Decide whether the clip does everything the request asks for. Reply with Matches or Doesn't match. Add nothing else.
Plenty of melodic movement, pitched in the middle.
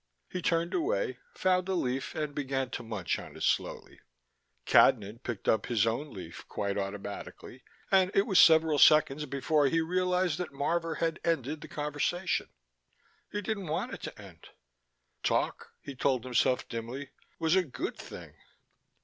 Matches